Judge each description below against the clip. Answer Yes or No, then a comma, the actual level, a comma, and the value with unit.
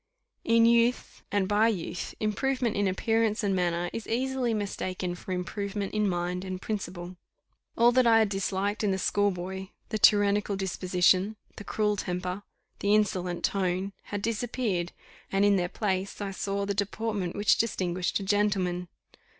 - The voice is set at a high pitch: Yes, high, 200 Hz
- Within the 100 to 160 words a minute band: Yes, average, 155 wpm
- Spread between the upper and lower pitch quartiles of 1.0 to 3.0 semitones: Yes, narrow, 2.6 semitones